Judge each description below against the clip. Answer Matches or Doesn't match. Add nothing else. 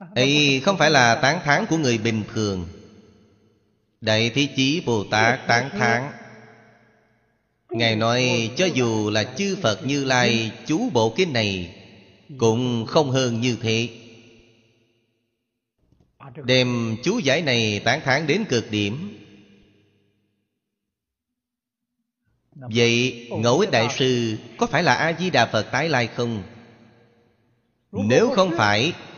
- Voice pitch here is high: Doesn't match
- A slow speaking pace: Matches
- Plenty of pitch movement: Doesn't match